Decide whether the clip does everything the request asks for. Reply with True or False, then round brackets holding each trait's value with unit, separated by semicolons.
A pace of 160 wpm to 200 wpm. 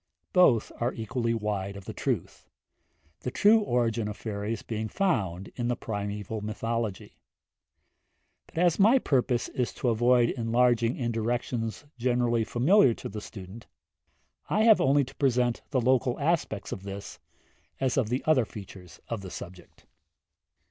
False (150 wpm)